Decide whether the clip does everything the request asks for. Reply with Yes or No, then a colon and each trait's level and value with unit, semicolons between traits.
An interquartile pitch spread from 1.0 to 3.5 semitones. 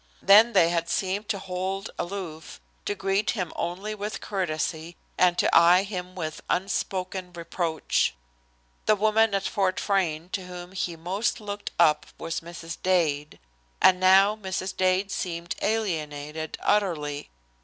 Yes: average, 2.8 semitones